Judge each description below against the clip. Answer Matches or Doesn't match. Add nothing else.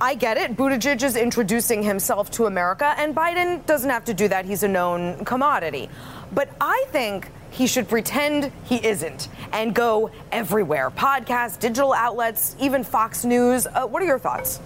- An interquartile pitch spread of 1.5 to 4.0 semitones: Doesn't match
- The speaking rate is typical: Matches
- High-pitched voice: Matches